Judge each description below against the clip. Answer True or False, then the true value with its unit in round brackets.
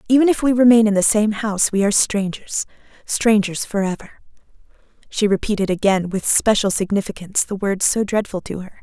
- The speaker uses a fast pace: False (165 wpm)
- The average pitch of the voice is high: True (205 Hz)